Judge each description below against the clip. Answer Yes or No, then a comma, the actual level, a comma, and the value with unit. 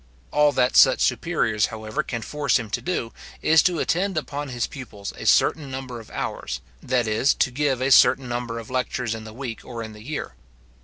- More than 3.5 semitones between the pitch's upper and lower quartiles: Yes, average, 3.9 semitones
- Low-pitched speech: Yes, low, 125 Hz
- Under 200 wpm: No, fast, 205 wpm